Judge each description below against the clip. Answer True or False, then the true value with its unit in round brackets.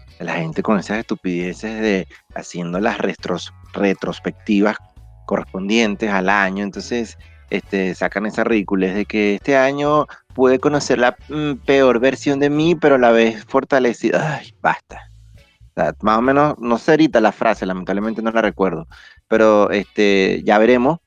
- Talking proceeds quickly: False (155 wpm)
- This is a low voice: True (110 Hz)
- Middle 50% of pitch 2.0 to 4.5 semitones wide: False (5.1 semitones)